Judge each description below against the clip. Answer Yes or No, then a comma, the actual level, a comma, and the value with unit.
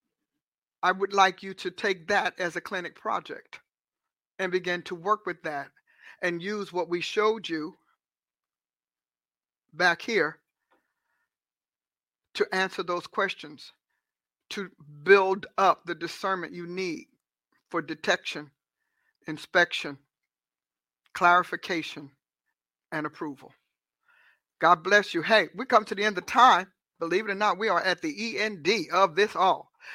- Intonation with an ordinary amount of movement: No, wide, 6.1 semitones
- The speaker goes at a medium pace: No, slow, 130 wpm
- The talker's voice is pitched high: No, medium, 180 Hz